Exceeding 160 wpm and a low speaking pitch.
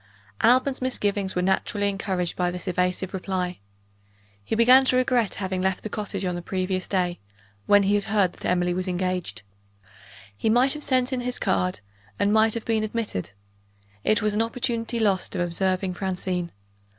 No: average, 175 wpm; high, 195 Hz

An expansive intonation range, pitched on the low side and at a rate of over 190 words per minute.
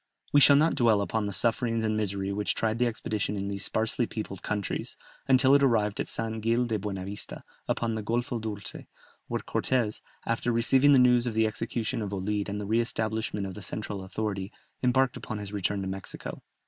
No: narrow, 2.6 semitones; low, 110 Hz; average, 200 wpm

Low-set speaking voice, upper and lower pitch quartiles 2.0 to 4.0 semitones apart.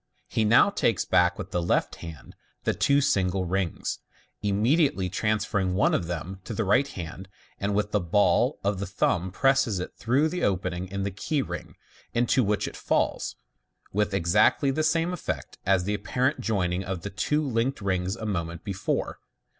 No: low, 100 Hz; average, 4.8 semitones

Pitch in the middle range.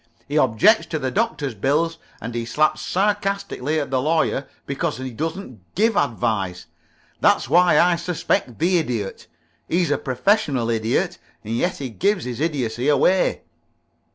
Yes: medium, 145 Hz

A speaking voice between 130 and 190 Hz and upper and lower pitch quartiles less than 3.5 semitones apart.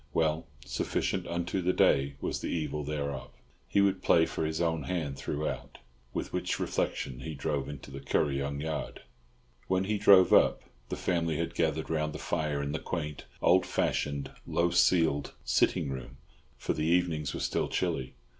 No: very low, 75 Hz; average, 3.1 semitones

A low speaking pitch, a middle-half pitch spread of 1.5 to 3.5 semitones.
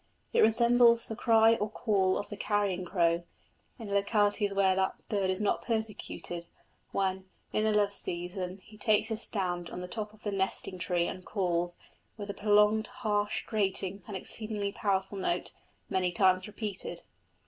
No: high, 200 Hz; narrow, 2.4 semitones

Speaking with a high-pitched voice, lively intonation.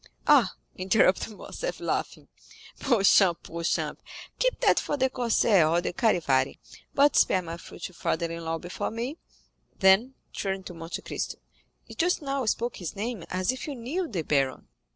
Yes: high, 195 Hz; wide, 7.0 semitones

